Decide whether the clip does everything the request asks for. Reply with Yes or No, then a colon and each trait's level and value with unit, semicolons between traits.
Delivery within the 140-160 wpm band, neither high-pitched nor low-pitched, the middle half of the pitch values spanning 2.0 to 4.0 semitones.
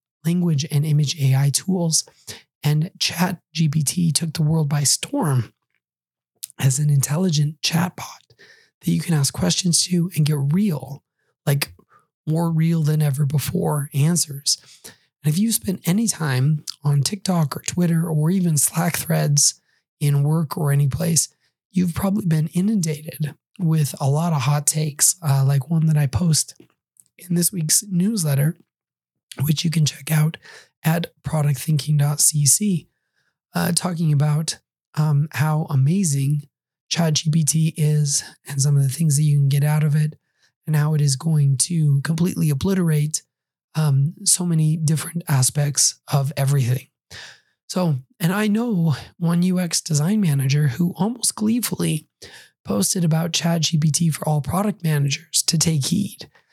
Yes: average, 145 wpm; medium, 155 Hz; average, 2.7 semitones